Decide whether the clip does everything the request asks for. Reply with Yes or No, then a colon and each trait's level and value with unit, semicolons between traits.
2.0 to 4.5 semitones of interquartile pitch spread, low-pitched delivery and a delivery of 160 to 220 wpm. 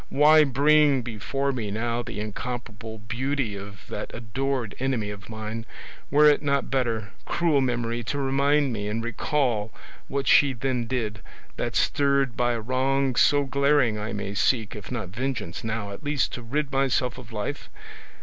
Yes: average, 3.9 semitones; low, 125 Hz; average, 165 wpm